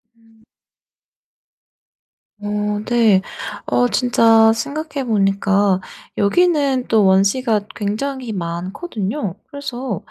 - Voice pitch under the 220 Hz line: No, high, 225 Hz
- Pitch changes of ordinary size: Yes, average, 4.5 semitones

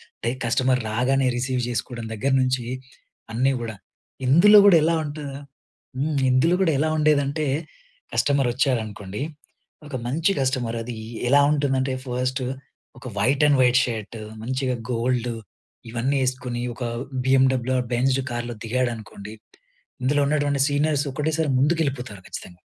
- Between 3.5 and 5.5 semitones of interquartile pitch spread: No, average, 2.8 semitones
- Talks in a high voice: No, low, 130 Hz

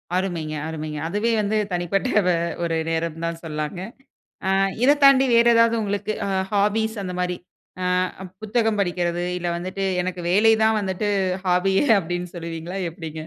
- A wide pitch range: No, average, 3.6 semitones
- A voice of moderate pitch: Yes, medium, 180 Hz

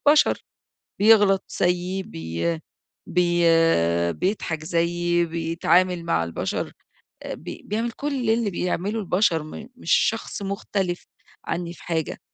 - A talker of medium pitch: Yes, medium, 180 Hz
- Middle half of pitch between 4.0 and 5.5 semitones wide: No, average, 3.5 semitones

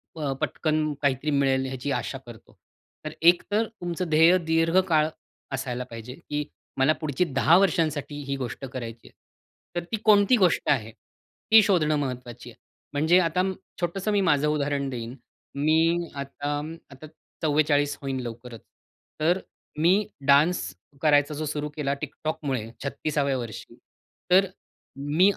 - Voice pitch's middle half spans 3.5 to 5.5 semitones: Yes, average, 3.8 semitones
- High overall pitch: No, medium, 150 Hz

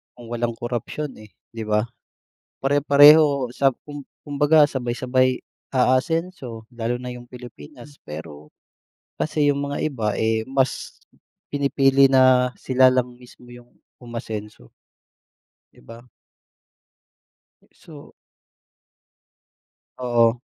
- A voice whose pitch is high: No, low, 125 Hz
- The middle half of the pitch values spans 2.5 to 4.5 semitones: Yes, average, 3.0 semitones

